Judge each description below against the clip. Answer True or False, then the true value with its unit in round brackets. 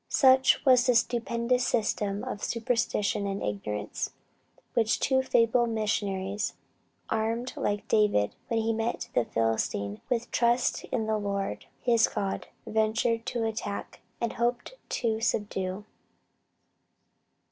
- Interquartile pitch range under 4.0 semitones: True (2.9 semitones)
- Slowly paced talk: True (120 wpm)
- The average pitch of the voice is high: True (225 Hz)